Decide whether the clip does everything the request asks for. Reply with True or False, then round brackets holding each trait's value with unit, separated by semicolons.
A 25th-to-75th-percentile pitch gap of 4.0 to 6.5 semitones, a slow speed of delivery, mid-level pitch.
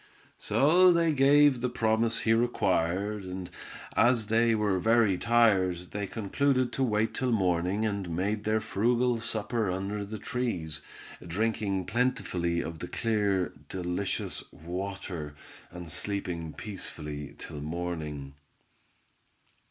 False (4.7 semitones; 120 wpm; 100 Hz)